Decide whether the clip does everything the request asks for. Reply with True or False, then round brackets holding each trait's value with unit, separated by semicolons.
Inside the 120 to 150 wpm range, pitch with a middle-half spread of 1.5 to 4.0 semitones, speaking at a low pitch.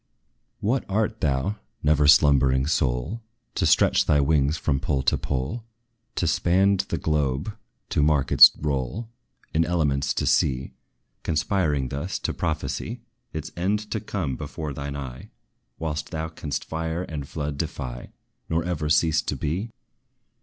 True (145 wpm; 3.7 semitones; 75 Hz)